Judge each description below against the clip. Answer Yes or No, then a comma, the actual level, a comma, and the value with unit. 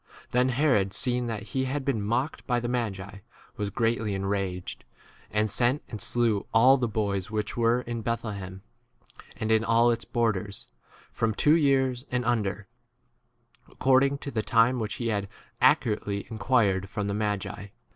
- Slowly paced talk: No, average, 175 wpm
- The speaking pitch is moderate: No, low, 115 Hz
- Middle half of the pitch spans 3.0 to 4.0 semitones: Yes, average, 3.3 semitones